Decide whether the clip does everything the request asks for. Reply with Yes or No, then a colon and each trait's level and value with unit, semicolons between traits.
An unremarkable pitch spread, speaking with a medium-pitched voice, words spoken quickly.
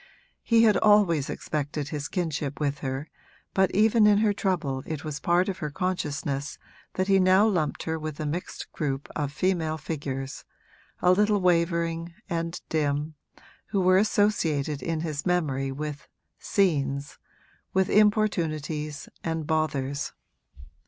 No: average, 4.3 semitones; medium, 160 Hz; average, 140 wpm